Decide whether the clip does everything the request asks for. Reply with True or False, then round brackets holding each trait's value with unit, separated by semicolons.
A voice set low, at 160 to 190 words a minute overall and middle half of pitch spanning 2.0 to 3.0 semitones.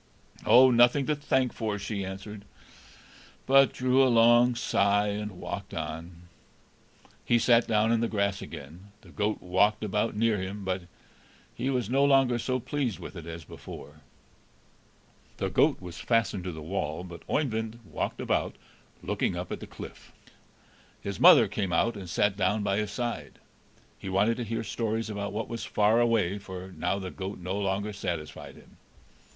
False (105 Hz; 170 wpm; 3.7 semitones)